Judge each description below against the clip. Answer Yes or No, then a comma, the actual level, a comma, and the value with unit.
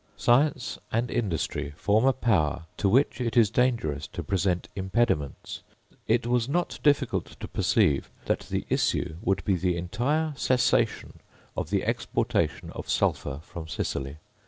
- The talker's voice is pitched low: Yes, low, 105 Hz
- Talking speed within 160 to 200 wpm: No, average, 145 wpm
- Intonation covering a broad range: Yes, wide, 6.5 semitones